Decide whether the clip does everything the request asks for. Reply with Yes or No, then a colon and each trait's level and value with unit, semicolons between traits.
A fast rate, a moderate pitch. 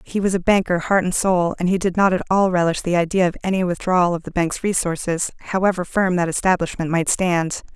Yes: fast, 225 wpm; medium, 180 Hz